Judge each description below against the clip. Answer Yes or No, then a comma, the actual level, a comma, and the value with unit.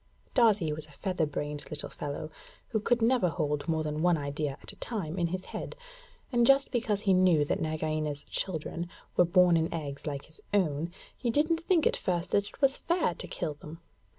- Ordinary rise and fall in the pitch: No, wide, 5.7 semitones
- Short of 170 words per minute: No, fast, 205 wpm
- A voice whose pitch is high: No, medium, 170 Hz